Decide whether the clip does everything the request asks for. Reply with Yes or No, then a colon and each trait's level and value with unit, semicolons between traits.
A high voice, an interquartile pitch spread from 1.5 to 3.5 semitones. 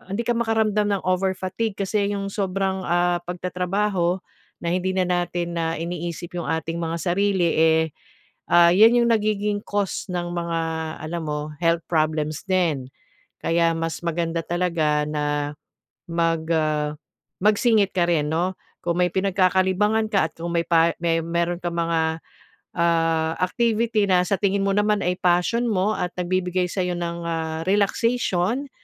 No: medium, 175 Hz; average, 2.9 semitones